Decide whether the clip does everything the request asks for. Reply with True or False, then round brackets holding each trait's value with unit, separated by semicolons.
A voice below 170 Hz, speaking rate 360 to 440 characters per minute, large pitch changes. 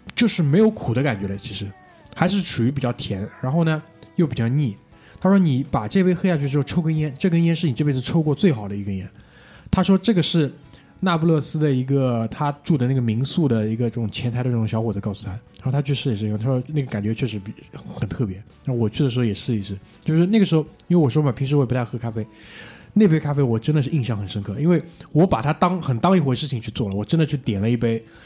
True (140 Hz; 370 characters per minute; 6.0 semitones)